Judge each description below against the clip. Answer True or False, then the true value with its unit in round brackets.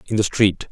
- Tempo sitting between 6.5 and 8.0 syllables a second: False (5.5 syllables/s)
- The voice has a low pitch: True (100 Hz)